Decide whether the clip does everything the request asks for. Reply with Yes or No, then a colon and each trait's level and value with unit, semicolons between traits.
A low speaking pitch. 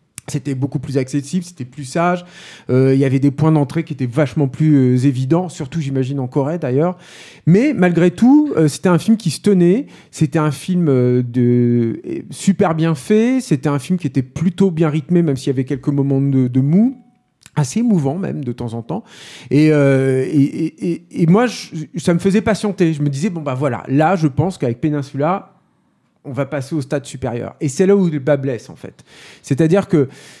No: medium, 155 Hz